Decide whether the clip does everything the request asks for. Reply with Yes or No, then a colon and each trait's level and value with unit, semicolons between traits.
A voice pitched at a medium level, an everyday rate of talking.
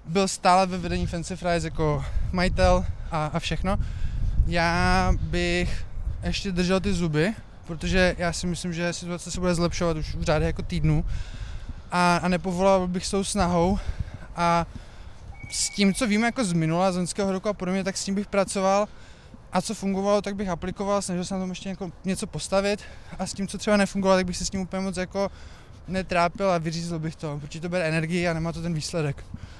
No: medium, 175 Hz; fast, 195 wpm